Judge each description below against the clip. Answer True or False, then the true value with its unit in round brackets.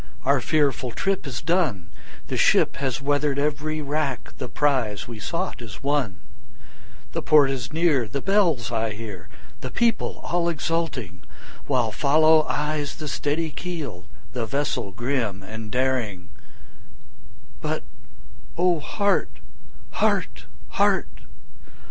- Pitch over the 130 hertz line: True (140 Hz)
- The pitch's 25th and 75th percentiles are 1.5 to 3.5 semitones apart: False (5.2 semitones)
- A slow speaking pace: True (125 wpm)